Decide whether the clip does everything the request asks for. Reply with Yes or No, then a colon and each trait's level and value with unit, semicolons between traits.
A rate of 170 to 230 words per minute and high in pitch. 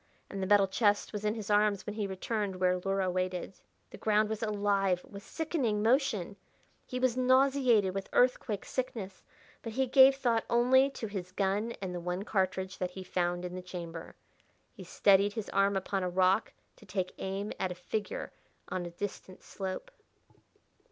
Yes: average, 180 wpm; high, 200 Hz